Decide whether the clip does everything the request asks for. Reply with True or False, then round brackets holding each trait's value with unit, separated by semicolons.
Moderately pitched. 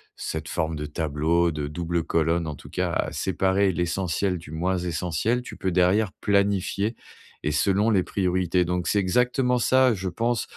False (90 Hz)